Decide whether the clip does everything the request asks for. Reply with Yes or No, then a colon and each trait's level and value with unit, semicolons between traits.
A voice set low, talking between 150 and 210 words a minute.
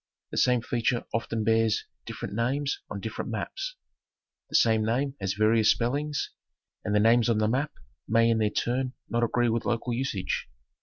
Yes: low, 115 Hz; average, 170 wpm